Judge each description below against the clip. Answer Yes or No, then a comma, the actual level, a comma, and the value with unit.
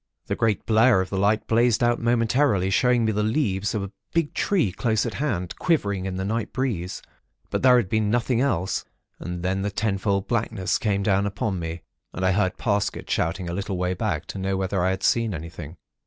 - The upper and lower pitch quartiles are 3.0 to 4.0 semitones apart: Yes, average, 3.6 semitones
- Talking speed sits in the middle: No, fast, 215 wpm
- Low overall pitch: Yes, low, 100 Hz